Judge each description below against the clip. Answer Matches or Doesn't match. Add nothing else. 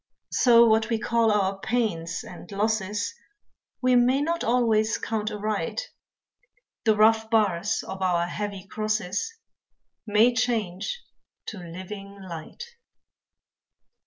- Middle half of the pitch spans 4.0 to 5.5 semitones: Doesn't match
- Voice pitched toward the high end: Matches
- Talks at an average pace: Doesn't match